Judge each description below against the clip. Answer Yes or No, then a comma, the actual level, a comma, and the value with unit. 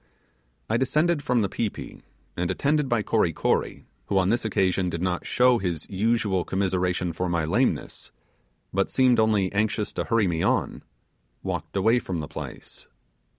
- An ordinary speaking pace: Yes, average, 165 wpm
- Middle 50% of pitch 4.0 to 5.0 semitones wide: Yes, average, 4.3 semitones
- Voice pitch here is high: No, low, 100 Hz